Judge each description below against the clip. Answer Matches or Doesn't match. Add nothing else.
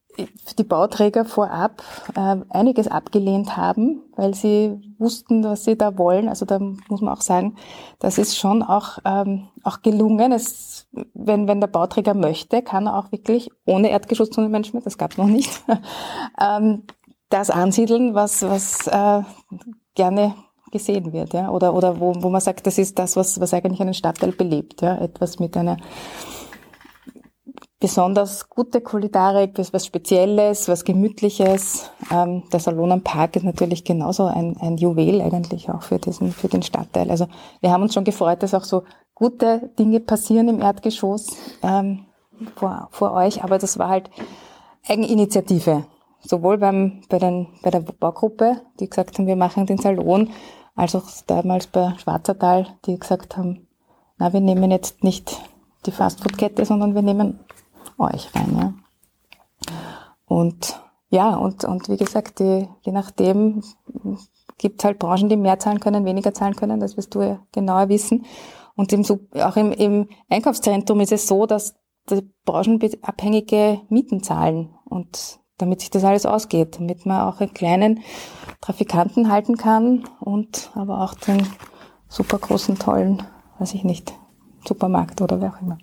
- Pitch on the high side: Matches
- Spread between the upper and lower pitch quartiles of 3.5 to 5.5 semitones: Doesn't match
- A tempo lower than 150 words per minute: Doesn't match